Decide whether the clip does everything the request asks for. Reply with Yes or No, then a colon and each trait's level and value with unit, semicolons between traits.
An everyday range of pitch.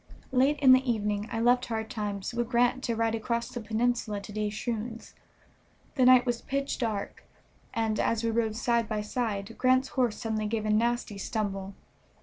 No: narrow, 2.3 semitones